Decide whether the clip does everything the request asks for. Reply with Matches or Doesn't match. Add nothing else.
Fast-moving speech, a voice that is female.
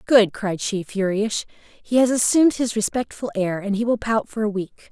Doesn't match